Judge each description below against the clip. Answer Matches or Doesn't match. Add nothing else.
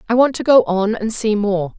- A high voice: Matches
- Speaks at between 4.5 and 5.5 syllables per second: Matches